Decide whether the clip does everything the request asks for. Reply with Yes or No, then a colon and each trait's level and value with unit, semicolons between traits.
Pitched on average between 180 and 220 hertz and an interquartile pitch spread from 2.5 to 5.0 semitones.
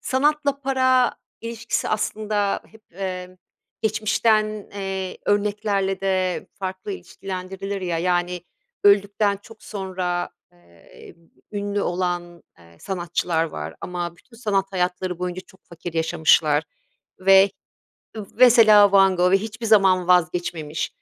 Yes: high, 190 Hz; average, 2.9 semitones